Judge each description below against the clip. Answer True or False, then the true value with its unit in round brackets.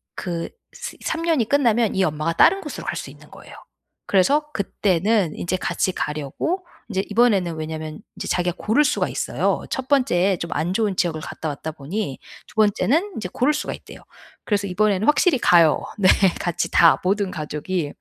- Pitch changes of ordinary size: False (6.0 semitones)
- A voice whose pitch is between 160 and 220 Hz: True (190 Hz)